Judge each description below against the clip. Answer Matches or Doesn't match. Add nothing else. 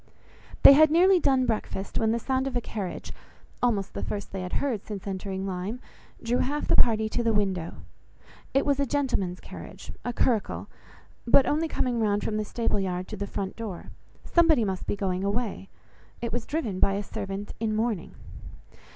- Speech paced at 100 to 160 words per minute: Doesn't match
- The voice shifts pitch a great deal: Doesn't match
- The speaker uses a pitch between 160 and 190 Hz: Doesn't match